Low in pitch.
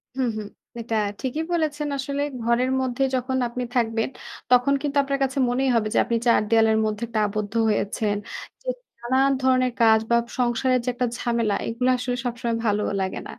No: high, 245 Hz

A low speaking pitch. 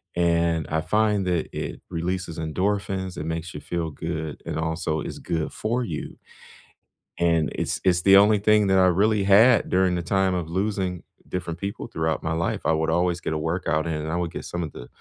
Yes: very low, 85 Hz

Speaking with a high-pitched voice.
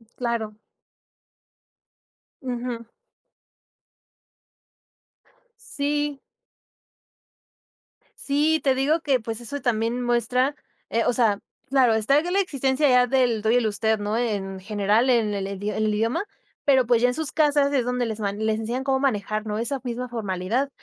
Yes: high, 240 Hz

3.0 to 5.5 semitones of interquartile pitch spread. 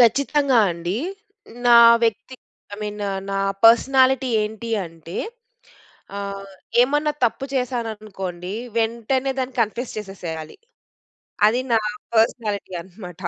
Yes: average, 4.3 semitones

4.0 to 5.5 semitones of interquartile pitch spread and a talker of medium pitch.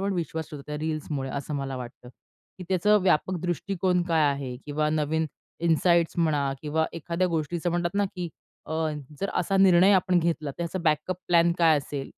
No: average, 2.9 semitones; medium, 165 Hz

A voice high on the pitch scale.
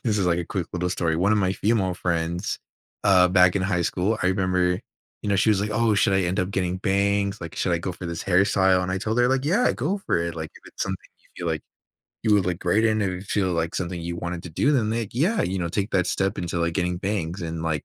No: very low, 95 Hz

